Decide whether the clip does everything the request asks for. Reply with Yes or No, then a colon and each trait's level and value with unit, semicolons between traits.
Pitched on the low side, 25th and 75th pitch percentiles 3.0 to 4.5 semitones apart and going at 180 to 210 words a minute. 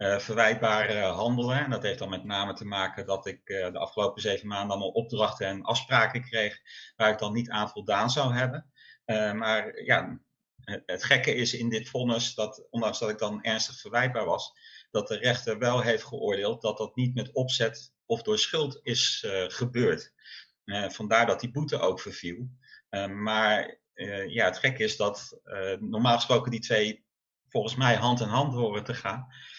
Yes: low, 115 Hz; average, 3.3 semitones; average, 190 wpm